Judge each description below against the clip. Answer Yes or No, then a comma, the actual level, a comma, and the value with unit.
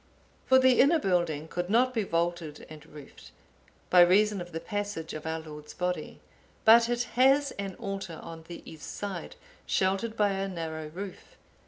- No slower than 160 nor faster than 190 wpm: Yes, average, 170 wpm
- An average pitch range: Yes, average, 4.6 semitones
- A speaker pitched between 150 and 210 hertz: Yes, medium, 185 Hz